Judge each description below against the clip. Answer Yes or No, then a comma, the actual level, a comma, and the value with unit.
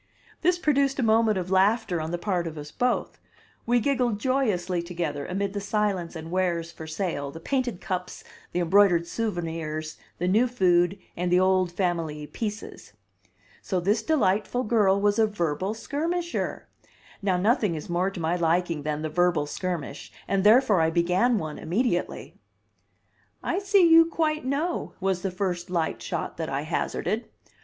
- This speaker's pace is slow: No, average, 165 wpm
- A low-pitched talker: No, medium, 185 Hz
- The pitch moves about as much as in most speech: Yes, average, 4.8 semitones